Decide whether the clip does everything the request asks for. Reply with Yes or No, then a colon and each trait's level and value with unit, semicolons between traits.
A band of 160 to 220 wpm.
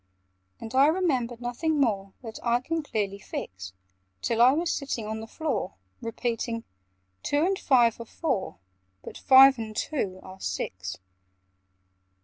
No: average, 140 wpm